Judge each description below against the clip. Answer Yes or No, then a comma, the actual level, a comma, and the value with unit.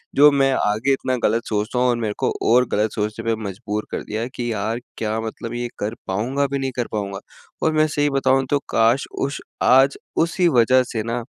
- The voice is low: Yes, low, 120 Hz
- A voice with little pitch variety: No, average, 3.7 semitones